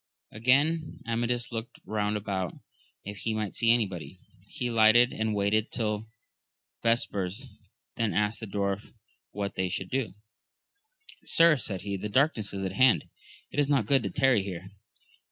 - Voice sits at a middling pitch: No, low, 110 Hz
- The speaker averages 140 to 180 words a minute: Yes, average, 155 wpm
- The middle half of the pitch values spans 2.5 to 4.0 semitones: Yes, average, 3.4 semitones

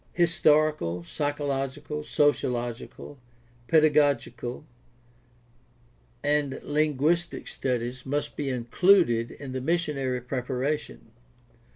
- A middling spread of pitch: Yes, average, 3.3 semitones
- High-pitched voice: No, medium, 140 Hz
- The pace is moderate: No, slow, 75 wpm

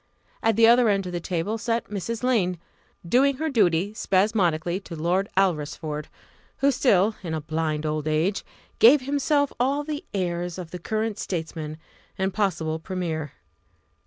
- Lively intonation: Yes, wide, 5.7 semitones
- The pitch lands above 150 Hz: Yes, high, 190 Hz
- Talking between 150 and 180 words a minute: Yes, average, 155 wpm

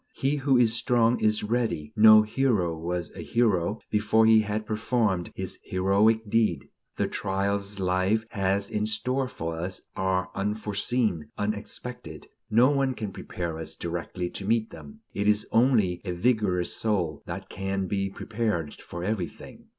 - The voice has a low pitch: Yes, low, 105 Hz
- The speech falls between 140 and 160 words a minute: Yes, average, 150 wpm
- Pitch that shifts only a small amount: No, average, 3.4 semitones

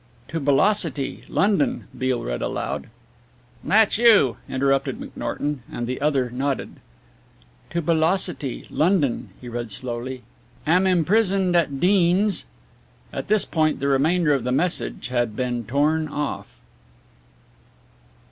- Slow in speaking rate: Yes, slow, 120 wpm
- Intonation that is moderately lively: No, wide, 5.7 semitones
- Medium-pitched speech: Yes, medium, 145 Hz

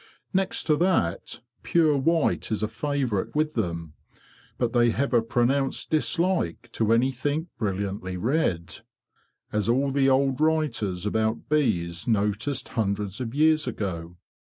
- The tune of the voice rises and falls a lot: Yes, wide, 6.0 semitones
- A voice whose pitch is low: Yes, low, 120 Hz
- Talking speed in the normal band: No, slow, 130 wpm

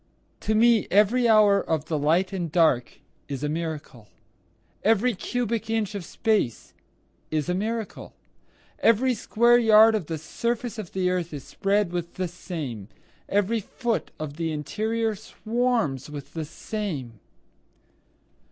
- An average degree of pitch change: No, wide, 5.9 semitones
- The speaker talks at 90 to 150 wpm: Yes, average, 140 wpm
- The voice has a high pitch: Yes, high, 195 Hz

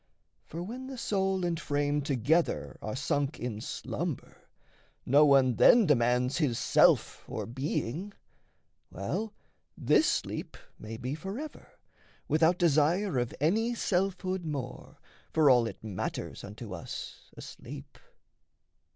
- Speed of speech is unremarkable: No, slow, 120 wpm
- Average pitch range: No, wide, 6.9 semitones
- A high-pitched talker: No, medium, 150 Hz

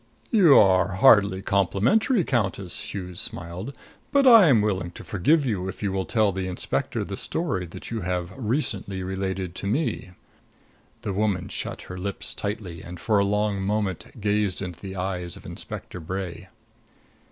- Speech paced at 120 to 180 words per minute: Yes, average, 165 wpm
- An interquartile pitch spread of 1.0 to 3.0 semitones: Yes, average, 2.7 semitones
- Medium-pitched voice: No, very low, 95 Hz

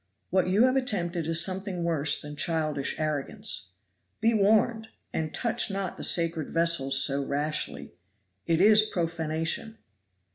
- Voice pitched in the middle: Yes, medium, 170 Hz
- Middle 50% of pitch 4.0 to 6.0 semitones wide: Yes, average, 4.8 semitones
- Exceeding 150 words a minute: No, slow, 135 wpm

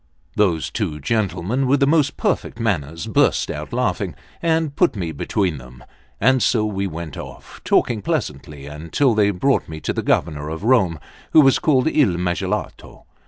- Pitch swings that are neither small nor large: No, wide, 8.5 semitones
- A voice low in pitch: Yes, low, 100 Hz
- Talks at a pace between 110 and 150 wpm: No, average, 165 wpm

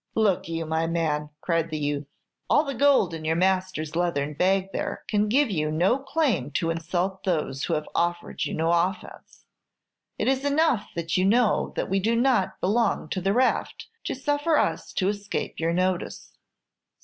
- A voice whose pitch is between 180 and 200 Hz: Yes, medium, 185 Hz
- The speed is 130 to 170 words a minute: No, average, 180 wpm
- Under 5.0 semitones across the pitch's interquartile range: No, wide, 5.5 semitones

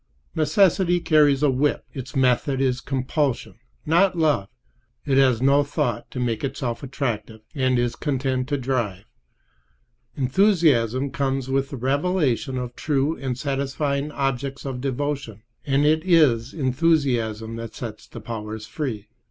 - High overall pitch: No, low, 135 Hz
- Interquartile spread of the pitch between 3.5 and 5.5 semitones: No, average, 3.0 semitones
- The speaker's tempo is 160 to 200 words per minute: No, slow, 135 wpm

